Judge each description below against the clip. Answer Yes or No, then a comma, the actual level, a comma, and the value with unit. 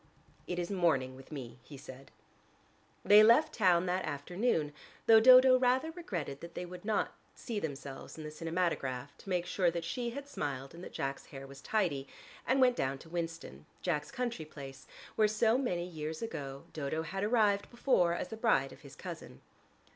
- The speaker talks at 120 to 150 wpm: No, average, 185 wpm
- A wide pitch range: Yes, wide, 7.4 semitones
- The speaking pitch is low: No, medium, 175 Hz